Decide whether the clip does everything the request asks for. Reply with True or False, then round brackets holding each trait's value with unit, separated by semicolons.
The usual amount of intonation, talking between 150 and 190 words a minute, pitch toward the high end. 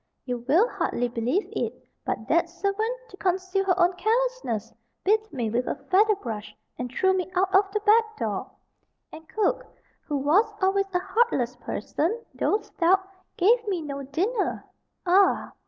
False (6.5 semitones; 160 wpm; 375 Hz)